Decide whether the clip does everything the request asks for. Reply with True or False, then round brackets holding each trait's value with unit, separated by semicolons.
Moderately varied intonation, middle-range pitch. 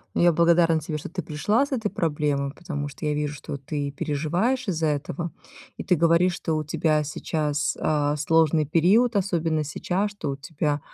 True (3.0 semitones; 155 Hz)